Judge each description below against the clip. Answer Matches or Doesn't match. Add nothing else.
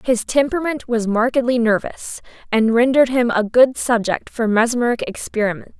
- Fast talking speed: Doesn't match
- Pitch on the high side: Matches